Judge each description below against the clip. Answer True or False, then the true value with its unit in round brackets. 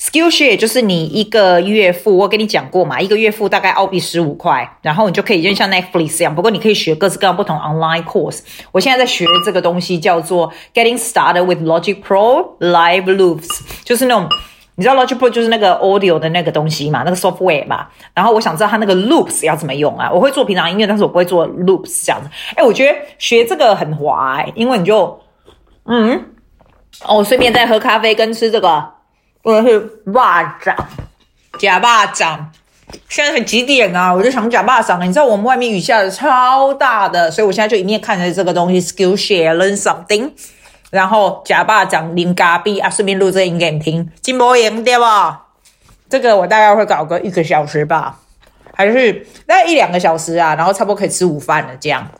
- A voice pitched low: False (195 Hz)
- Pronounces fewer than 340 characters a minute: False (405 characters per minute)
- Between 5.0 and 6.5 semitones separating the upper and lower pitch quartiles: False (4.6 semitones)